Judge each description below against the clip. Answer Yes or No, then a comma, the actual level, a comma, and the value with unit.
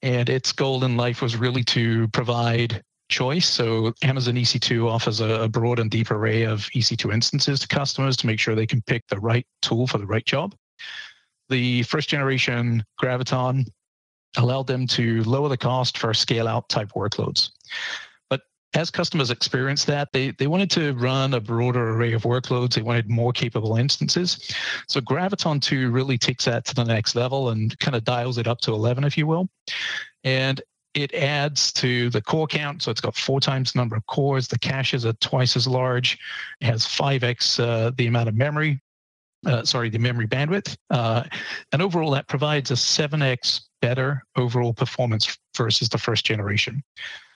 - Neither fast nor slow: Yes, average, 180 wpm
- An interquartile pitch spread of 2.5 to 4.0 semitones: Yes, average, 2.8 semitones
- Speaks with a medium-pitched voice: No, low, 125 Hz